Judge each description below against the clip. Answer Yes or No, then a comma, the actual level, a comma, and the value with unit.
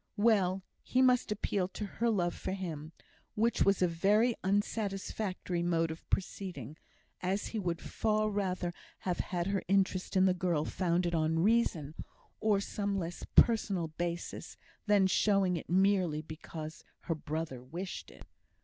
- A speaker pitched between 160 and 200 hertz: Yes, medium, 185 Hz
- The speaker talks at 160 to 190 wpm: No, average, 150 wpm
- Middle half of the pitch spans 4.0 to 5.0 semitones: No, average, 3.1 semitones